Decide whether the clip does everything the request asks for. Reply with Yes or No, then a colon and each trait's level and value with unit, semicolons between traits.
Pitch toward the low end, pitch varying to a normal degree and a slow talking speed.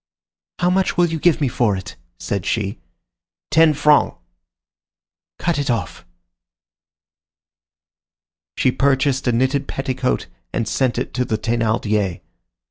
Yes: low, 130 Hz; average, 4.7 semitones; slow, 125 wpm